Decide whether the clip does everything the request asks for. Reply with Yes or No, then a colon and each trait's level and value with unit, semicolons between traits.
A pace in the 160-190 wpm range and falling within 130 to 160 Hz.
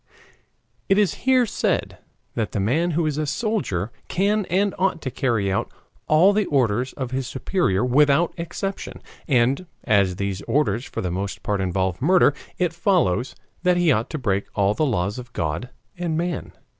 Yes: average, 175 wpm; low, 135 Hz